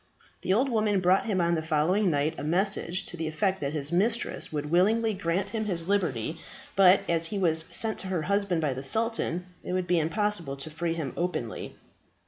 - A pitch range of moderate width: Yes, average, 3.9 semitones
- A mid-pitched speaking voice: Yes, medium, 175 Hz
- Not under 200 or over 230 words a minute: Yes, fast, 205 wpm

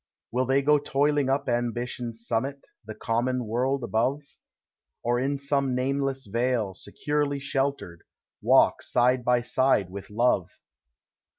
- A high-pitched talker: No, low, 125 Hz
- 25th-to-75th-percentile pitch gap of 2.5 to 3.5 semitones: Yes, average, 2.8 semitones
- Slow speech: Yes, slow, 125 wpm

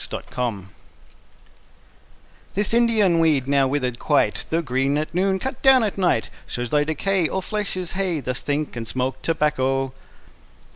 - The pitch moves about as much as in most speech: No, wide, 6.5 semitones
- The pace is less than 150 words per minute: No, average, 160 wpm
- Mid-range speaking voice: Yes, medium, 150 Hz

